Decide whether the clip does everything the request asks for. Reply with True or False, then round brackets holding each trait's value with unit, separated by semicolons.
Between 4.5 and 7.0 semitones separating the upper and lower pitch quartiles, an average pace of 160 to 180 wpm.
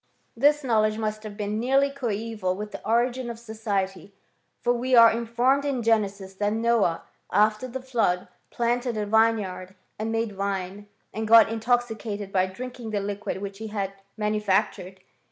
False (2.6 semitones; 165 wpm)